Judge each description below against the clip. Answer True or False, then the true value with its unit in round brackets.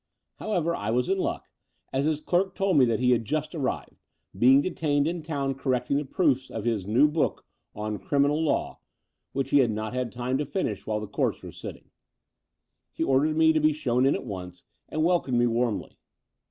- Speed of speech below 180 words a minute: False (205 wpm)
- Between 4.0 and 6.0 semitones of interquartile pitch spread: True (4.5 semitones)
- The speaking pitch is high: False (135 Hz)